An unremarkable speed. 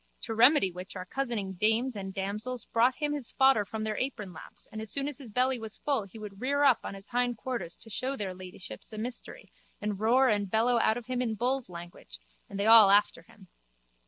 No: fast, 220 wpm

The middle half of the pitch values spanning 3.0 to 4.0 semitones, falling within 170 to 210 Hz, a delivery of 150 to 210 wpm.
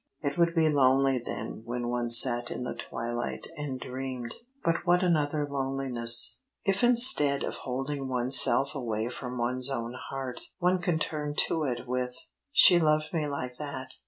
No: average, 3.5 semitones; low, 135 Hz; average, 165 wpm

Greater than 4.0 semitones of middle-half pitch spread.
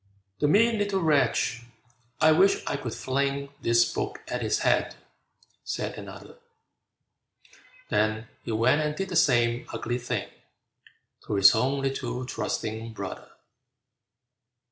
Yes: average, 4.8 semitones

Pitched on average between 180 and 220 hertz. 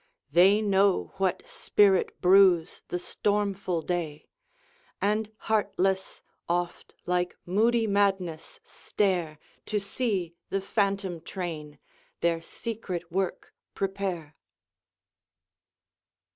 Yes: high, 190 Hz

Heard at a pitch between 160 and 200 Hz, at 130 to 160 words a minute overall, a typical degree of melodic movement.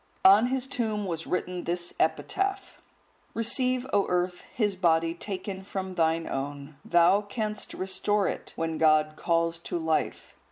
Yes: medium, 185 Hz; average, 145 wpm; average, 4.1 semitones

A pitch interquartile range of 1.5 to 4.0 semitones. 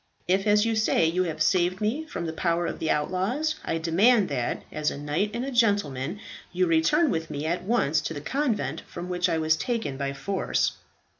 No: average, 5.1 semitones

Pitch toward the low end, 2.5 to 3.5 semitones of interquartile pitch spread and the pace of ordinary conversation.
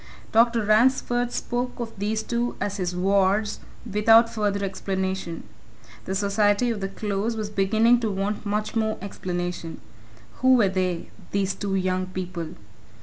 No: high, 205 Hz; average, 2.8 semitones; average, 145 wpm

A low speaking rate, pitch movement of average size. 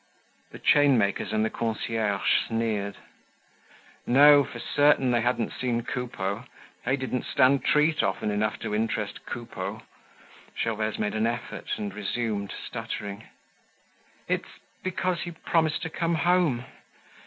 Yes: slow, 125 wpm; average, 4.9 semitones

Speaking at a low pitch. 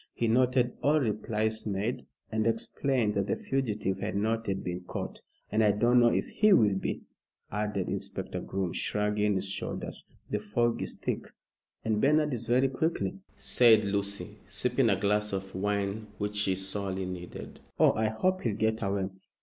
Yes: low, 105 Hz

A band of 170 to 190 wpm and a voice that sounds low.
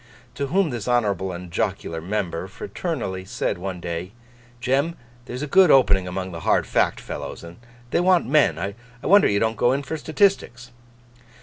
Yes: average, 175 wpm; low, 115 Hz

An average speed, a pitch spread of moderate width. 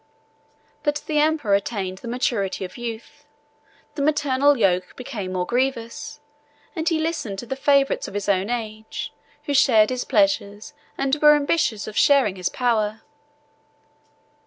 No: average, 145 wpm; wide, 5.7 semitones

